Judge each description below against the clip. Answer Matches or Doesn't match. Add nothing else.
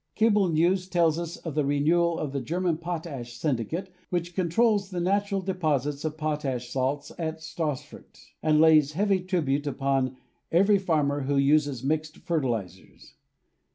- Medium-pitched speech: Matches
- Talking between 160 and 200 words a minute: Doesn't match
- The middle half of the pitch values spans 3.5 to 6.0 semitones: Matches